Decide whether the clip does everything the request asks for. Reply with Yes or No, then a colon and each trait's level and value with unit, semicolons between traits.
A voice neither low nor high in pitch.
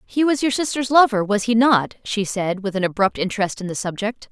No: high, 220 Hz